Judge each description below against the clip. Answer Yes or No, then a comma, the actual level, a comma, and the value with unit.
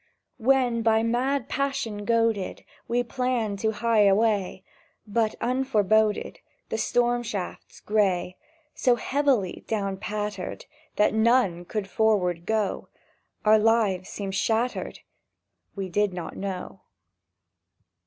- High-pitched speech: Yes, high, 220 Hz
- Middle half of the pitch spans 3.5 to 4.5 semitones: No, average, 3.0 semitones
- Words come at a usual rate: No, slow, 110 wpm